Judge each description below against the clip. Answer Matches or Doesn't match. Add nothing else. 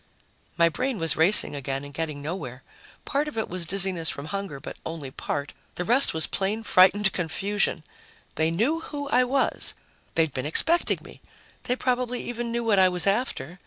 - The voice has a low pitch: Doesn't match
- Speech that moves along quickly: Doesn't match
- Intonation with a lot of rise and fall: Matches